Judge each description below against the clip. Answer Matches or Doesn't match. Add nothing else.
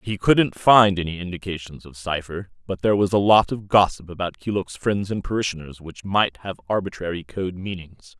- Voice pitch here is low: Matches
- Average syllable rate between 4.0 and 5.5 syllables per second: Matches